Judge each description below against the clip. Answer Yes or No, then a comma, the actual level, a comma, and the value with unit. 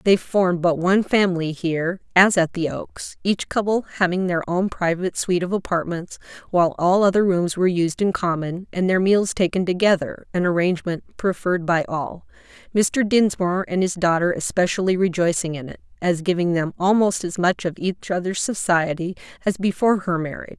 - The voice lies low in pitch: No, medium, 180 Hz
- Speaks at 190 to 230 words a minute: No, average, 175 wpm